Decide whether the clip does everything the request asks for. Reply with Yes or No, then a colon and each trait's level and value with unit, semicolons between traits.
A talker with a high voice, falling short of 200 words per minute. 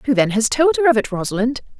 No: very high, 250 Hz; fast, 265 wpm